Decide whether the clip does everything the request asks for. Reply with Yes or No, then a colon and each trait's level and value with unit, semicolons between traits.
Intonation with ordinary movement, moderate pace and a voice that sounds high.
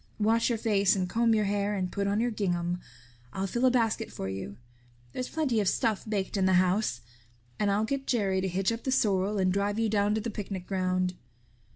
No: average, 3.1 semitones; fast, 220 wpm; high, 205 Hz